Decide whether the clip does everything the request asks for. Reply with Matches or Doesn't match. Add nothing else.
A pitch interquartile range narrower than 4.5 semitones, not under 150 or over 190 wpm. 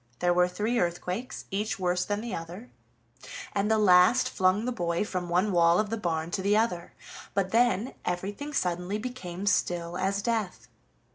Matches